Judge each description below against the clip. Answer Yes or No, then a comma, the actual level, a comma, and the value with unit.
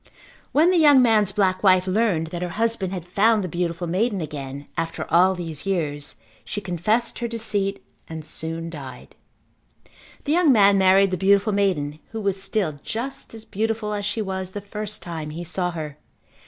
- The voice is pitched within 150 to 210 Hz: Yes, high, 190 Hz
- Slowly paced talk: No, average, 180 wpm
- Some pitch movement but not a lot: Yes, average, 4.2 semitones